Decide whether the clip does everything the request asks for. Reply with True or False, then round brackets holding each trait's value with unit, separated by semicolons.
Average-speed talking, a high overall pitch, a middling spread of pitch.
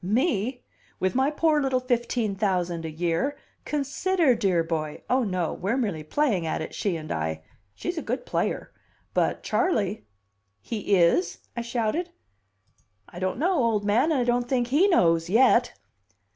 False (165 wpm; 220 Hz; 7.1 semitones)